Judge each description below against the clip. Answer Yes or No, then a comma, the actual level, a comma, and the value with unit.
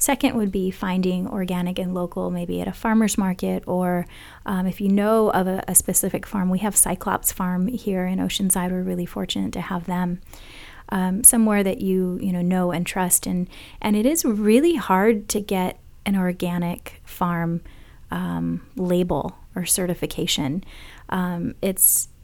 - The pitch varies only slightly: Yes, narrow, 2.2 semitones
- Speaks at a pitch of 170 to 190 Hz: Yes, medium, 185 Hz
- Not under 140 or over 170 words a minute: Yes, average, 165 wpm